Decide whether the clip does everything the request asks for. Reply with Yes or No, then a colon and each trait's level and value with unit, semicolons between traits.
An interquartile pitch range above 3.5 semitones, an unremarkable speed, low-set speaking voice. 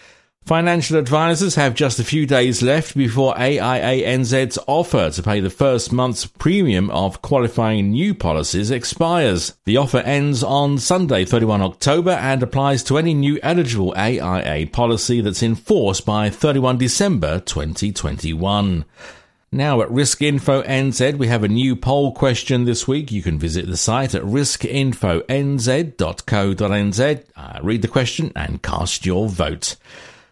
Yes: wide, 5.6 semitones; average, 145 wpm; low, 125 Hz